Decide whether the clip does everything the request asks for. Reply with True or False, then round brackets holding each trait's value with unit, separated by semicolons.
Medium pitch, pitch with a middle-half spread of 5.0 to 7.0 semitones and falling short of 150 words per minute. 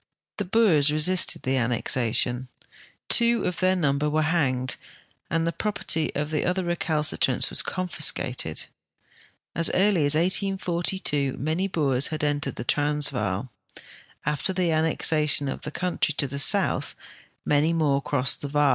False (150 Hz; 3.7 semitones; 140 wpm)